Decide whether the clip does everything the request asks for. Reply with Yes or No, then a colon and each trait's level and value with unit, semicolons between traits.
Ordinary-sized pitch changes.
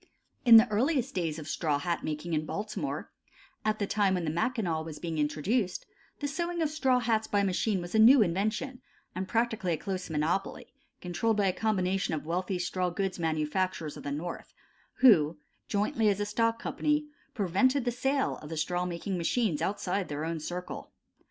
Yes: average, 5.0 semitones